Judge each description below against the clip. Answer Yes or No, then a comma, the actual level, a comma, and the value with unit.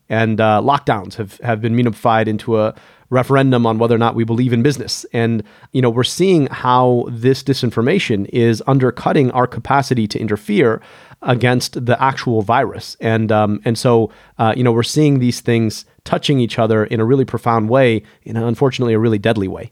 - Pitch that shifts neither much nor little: No, narrow, 2.2 semitones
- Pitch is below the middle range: Yes, low, 120 Hz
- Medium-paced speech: Yes, average, 190 wpm